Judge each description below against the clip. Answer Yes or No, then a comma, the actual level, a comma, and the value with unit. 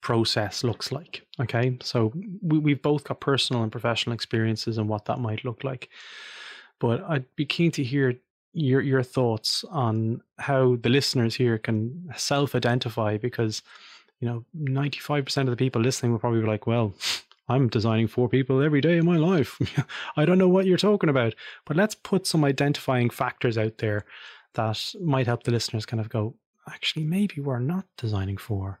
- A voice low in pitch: Yes, low, 125 Hz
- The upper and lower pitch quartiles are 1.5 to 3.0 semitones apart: No, average, 4.0 semitones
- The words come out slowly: No, average, 185 wpm